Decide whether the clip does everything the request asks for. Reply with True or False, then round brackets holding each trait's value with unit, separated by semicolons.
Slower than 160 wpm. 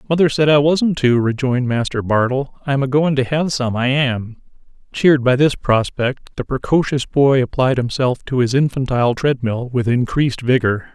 False (175 wpm)